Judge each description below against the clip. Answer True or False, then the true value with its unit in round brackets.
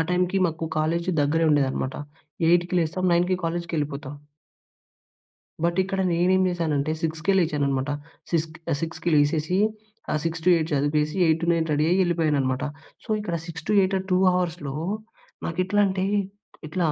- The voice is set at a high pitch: False (165 Hz)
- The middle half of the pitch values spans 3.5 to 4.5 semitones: False (2.9 semitones)